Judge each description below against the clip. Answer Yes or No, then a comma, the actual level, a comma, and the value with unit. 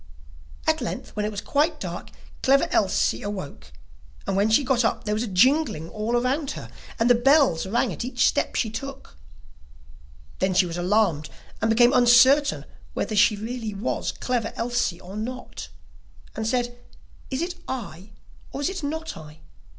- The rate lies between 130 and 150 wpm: No, average, 175 wpm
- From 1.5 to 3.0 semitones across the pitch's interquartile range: No, average, 4.3 semitones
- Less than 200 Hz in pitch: No, high, 230 Hz